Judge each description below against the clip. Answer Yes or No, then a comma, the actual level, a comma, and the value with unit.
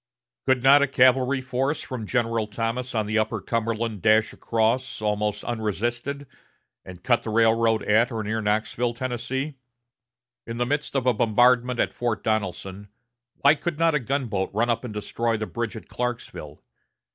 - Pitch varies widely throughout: No, average, 2.7 semitones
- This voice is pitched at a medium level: No, low, 115 Hz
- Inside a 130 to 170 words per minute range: Yes, average, 165 wpm